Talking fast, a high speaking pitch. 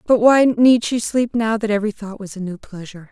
Yes: fast, 250 wpm; high, 215 Hz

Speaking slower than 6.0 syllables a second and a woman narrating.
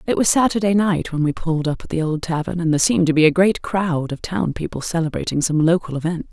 No: 6.3 syllables/s; female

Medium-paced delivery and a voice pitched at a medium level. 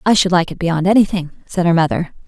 No: fast, 235 wpm; medium, 175 Hz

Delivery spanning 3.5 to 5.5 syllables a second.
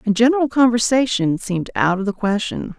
No: 5.7 syllables/s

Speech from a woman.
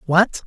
No: male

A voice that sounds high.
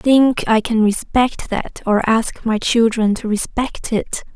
Yes: high, 225 Hz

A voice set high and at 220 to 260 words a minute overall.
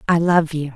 No: medium, 160 Hz; fast, 240 wpm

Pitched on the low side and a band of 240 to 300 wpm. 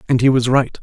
Yes: low, 125 Hz; fast, 290 wpm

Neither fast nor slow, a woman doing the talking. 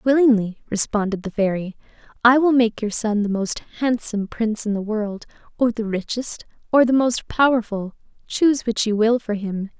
Yes: average, 180 wpm; female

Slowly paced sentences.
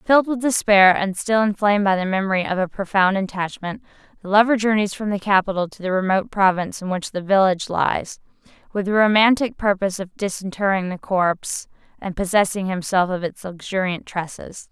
No: average, 175 wpm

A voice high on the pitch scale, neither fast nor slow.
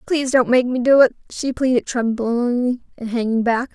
Yes: high, 245 Hz; average, 190 wpm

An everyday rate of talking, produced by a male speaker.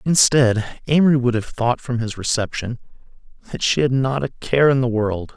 Yes: average, 190 wpm; male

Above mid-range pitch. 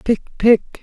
Yes: high, 225 Hz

